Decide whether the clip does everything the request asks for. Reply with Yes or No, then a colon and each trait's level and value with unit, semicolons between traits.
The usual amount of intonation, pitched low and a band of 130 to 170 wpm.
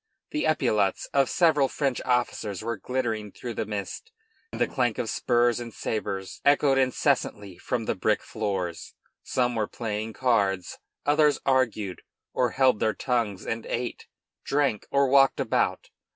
Yes: average, 4.0 semitones; low, 120 Hz; average, 150 wpm